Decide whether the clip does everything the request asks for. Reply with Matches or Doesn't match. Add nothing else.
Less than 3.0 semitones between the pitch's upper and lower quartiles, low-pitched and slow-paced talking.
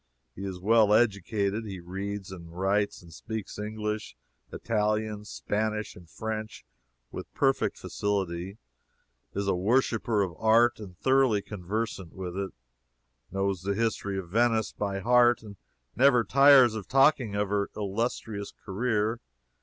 Matches